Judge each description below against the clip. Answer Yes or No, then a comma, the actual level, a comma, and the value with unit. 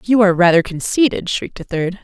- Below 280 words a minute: Yes, fast, 205 wpm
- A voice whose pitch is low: No, high, 190 Hz